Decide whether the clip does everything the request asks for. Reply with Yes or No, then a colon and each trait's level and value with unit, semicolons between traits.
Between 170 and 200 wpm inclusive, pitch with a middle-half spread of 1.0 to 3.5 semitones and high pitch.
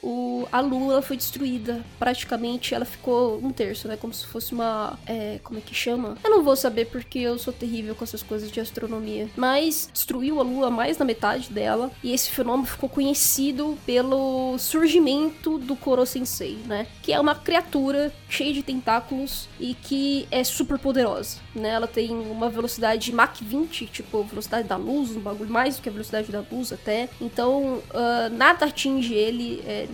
Yes: average, 180 wpm; average, 3.1 semitones; high, 245 Hz